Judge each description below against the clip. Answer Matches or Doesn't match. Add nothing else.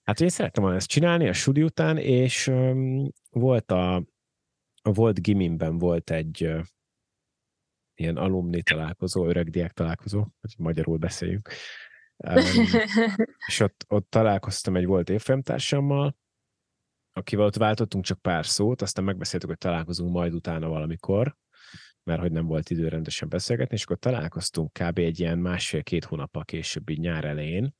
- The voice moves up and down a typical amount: Doesn't match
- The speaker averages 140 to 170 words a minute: Matches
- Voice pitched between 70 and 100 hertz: Matches